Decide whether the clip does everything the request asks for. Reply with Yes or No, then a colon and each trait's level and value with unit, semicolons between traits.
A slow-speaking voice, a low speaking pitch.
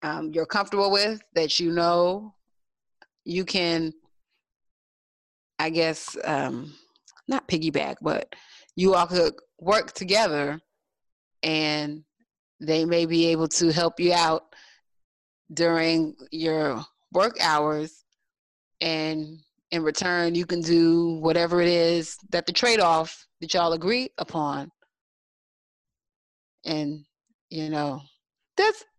No: slow, 110 wpm; medium, 165 Hz